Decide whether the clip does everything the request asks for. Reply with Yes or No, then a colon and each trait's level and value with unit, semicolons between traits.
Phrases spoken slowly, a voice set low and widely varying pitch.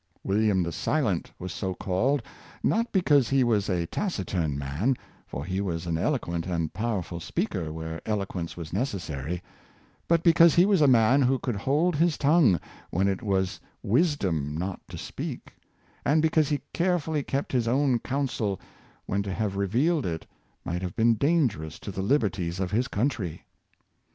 No: average, 165 wpm; low, 105 Hz; wide, 7.8 semitones